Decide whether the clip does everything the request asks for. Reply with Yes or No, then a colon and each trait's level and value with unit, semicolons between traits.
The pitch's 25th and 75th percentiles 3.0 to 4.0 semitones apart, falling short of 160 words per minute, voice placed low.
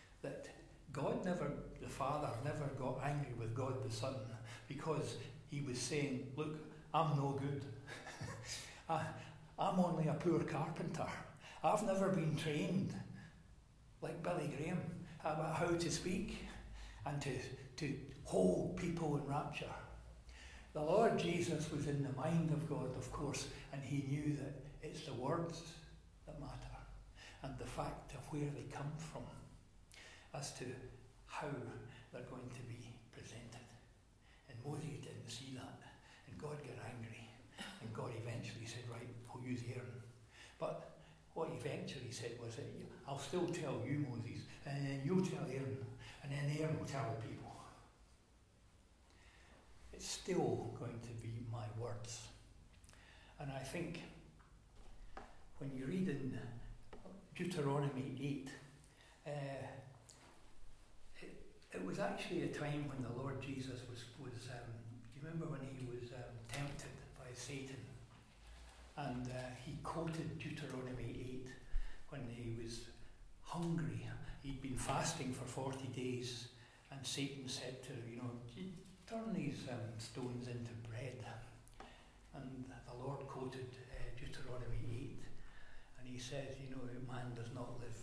Yes: average, 3.4 semitones; slow, 135 wpm; low, 130 Hz